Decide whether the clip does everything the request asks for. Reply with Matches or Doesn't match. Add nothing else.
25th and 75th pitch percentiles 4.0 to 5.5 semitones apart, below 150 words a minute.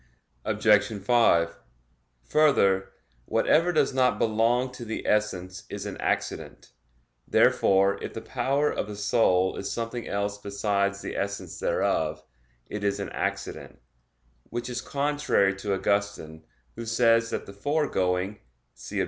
Doesn't match